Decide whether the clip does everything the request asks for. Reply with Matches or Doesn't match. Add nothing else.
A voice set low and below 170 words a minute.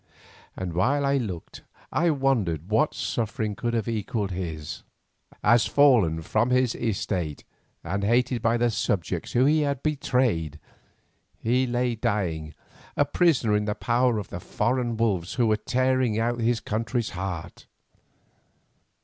Matches